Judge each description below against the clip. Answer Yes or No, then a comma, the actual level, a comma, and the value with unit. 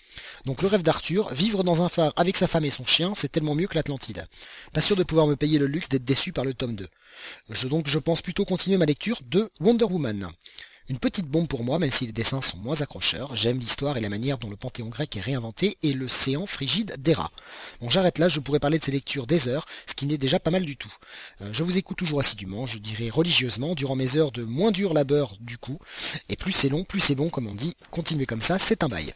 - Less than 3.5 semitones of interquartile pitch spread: No, average, 5.2 semitones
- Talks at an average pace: No, fast, 260 wpm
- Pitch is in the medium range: Yes, medium, 145 Hz